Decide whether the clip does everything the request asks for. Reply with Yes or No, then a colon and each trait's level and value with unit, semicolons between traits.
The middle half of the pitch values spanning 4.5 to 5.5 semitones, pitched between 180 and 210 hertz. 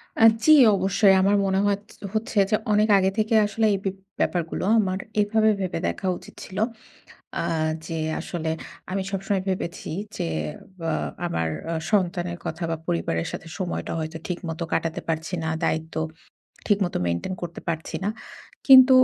No: average, 3.7 semitones; medium, 185 Hz